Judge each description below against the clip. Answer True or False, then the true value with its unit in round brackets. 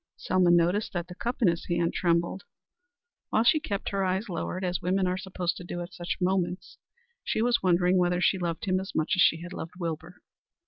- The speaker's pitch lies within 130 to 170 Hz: False (180 Hz)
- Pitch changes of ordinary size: False (1.7 semitones)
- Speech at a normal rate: False (215 wpm)